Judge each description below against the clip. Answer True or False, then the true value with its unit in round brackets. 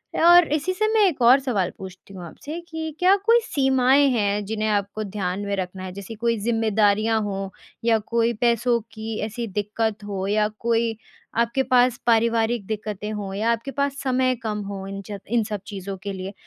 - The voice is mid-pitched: False (220 Hz)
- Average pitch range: True (3.4 semitones)